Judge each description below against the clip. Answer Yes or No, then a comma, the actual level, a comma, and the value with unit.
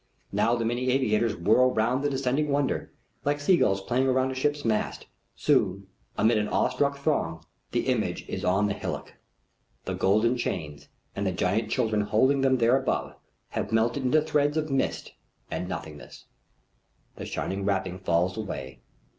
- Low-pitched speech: Yes, low, 115 Hz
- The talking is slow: No, average, 160 wpm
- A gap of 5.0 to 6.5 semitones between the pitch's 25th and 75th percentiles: Yes, average, 5.3 semitones